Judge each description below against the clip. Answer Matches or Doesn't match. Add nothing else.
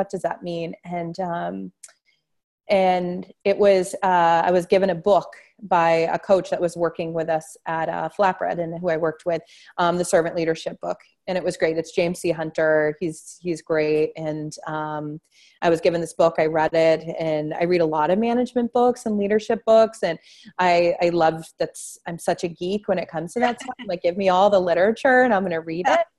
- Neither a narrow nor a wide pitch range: Matches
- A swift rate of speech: Matches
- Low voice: Doesn't match